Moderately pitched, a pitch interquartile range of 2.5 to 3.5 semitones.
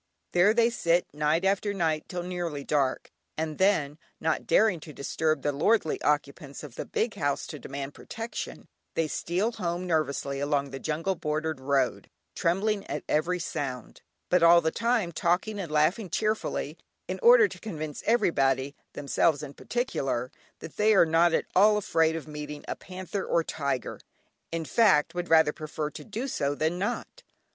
No: medium, 165 Hz; average, 4.5 semitones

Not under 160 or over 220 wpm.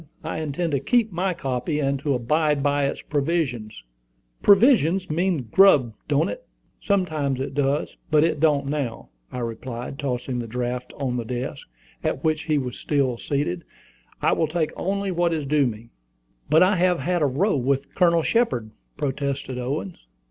Yes: average, 170 wpm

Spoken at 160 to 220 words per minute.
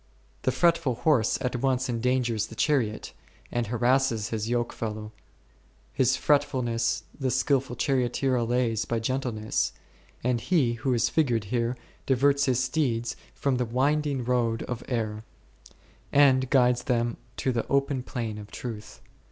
No: average, 145 wpm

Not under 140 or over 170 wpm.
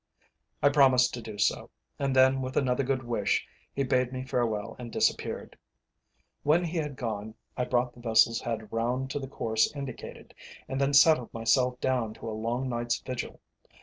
No: average, 180 wpm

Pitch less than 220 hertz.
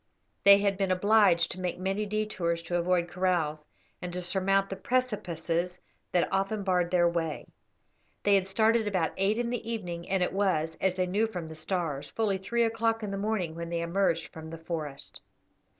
Yes: medium, 185 Hz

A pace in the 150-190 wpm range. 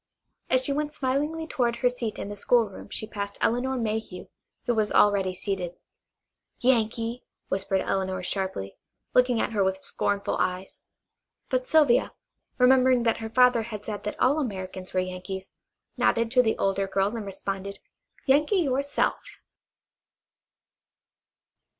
No: average, 140 wpm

